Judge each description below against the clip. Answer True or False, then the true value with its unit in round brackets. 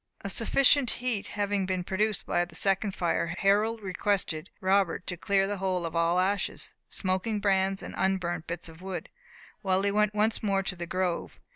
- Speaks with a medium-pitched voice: False (195 Hz)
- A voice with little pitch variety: True (2.1 semitones)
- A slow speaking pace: False (180 wpm)